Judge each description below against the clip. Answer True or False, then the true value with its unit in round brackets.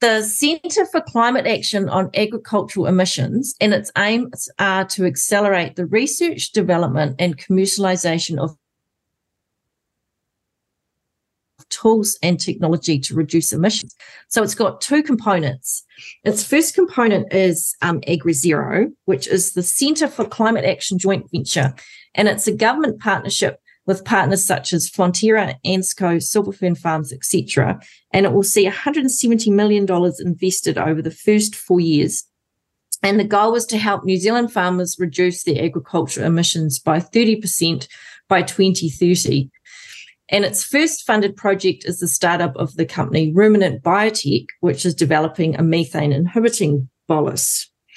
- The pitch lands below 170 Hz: False (185 Hz)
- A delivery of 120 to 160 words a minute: True (135 wpm)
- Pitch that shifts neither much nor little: True (4.2 semitones)